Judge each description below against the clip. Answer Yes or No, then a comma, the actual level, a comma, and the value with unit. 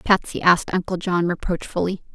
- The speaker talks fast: No, average, 140 wpm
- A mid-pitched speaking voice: Yes, medium, 180 Hz